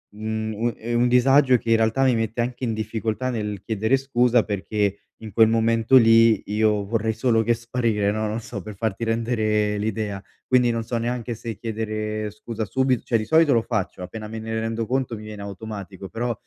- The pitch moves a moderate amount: No, narrow, 1.7 semitones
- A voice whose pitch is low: Yes, low, 110 Hz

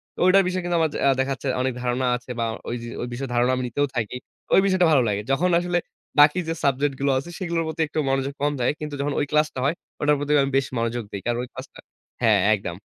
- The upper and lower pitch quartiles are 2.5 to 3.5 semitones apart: No, average, 4.2 semitones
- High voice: No, medium, 140 Hz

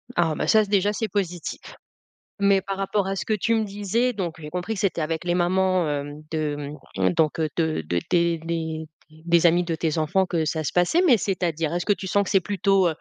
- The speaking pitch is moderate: Yes, medium, 175 Hz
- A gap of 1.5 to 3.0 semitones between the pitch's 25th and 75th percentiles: No, average, 3.6 semitones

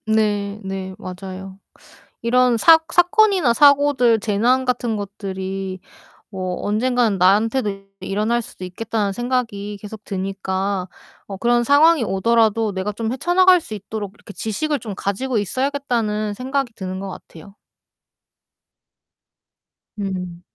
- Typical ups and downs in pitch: Yes, average, 4.3 semitones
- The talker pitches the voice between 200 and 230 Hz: Yes, high, 215 Hz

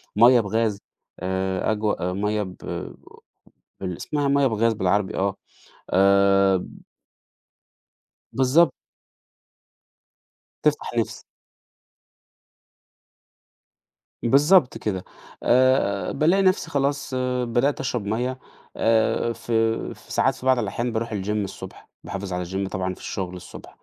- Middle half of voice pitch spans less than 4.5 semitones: No, average, 5.0 semitones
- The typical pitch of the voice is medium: No, low, 105 Hz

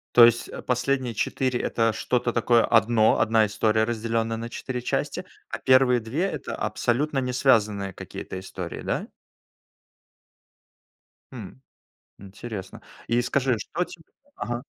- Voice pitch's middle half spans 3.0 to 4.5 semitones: No, narrow, 2.5 semitones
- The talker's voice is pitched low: Yes, low, 120 Hz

